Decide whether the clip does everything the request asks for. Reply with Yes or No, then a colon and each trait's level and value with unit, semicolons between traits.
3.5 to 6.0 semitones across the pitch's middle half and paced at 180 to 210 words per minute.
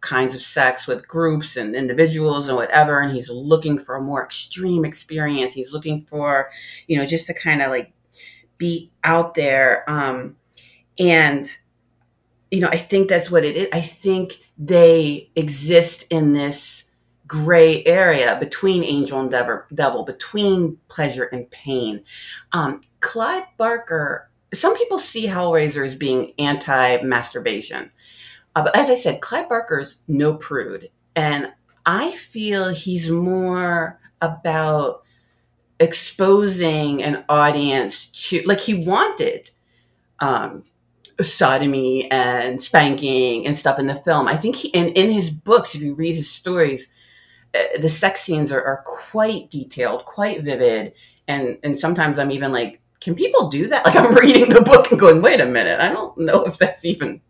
No: average, 4.7 semitones; average, 155 wpm